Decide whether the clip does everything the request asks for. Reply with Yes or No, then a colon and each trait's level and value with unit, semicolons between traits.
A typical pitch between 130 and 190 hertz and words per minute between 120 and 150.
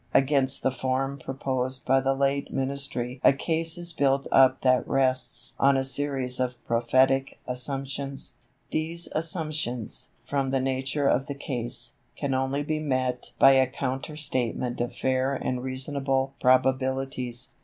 Yes: low, 135 Hz; average, 145 wpm